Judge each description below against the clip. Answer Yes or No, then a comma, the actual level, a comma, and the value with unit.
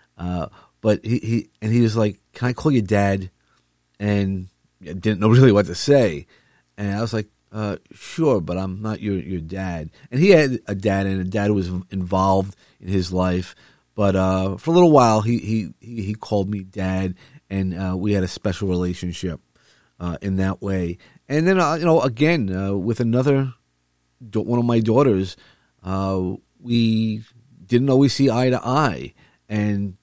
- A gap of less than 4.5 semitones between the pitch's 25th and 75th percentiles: Yes, average, 4.1 semitones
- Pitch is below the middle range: Yes, low, 100 Hz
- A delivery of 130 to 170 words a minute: No, average, 185 wpm